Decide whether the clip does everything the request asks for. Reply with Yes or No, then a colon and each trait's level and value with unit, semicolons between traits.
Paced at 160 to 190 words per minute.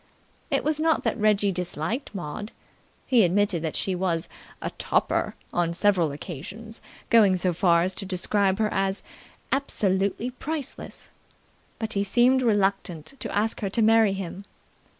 No: average, 150 wpm